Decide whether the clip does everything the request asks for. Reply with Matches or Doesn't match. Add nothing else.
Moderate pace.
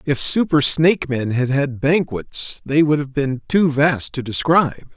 Matches